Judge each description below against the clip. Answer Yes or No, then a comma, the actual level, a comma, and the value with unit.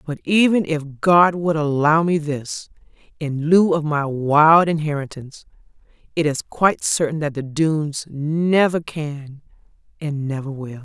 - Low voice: No, medium, 155 Hz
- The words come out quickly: No, average, 145 wpm